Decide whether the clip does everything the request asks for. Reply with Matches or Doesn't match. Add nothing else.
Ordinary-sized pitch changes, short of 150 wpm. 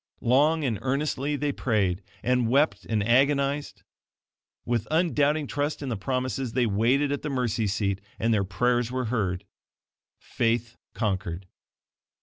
Matches